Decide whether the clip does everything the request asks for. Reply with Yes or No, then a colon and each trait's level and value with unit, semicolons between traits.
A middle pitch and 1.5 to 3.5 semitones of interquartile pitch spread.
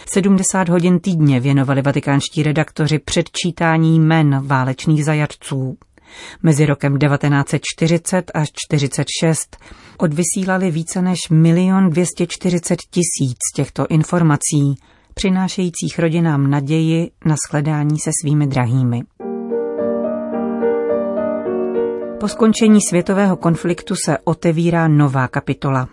No: medium, 155 Hz; average, 3.9 semitones